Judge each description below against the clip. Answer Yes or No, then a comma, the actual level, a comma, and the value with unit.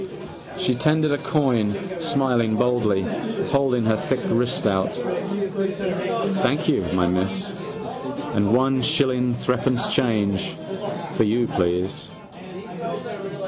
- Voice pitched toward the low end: Yes, low, 125 Hz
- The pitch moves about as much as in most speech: No, wide, 5.9 semitones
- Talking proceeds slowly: Yes, slow, 100 wpm